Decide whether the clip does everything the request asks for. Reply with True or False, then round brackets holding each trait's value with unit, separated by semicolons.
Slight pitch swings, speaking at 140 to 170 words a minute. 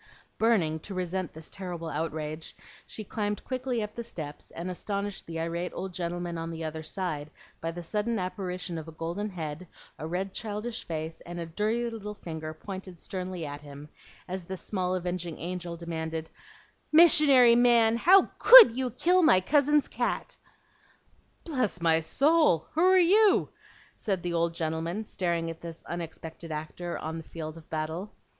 False (4.7 semitones; 165 wpm)